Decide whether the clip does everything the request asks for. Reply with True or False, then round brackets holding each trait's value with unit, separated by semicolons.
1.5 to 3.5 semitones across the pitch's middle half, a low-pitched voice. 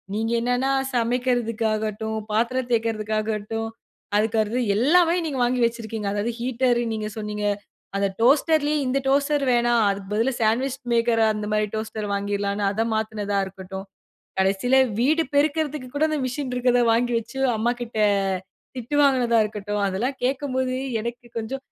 False (3.2 semitones; 235 Hz)